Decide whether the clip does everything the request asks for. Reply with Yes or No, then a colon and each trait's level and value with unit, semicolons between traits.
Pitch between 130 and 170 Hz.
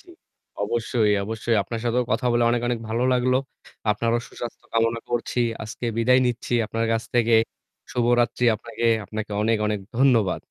No: low, 115 Hz